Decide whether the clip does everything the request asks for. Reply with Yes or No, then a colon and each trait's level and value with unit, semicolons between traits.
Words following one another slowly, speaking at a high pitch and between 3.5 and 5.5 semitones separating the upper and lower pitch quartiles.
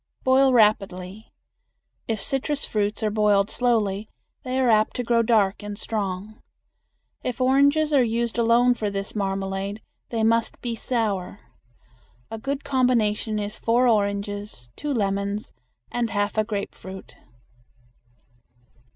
No: slow, 125 wpm; high, 220 Hz; average, 3.1 semitones